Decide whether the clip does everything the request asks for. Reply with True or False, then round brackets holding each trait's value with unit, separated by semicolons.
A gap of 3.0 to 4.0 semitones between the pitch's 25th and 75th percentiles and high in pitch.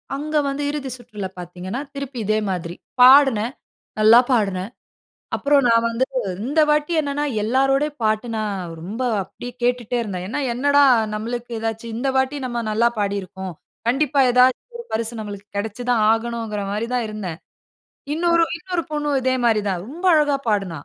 False (4.7 semitones; 235 Hz)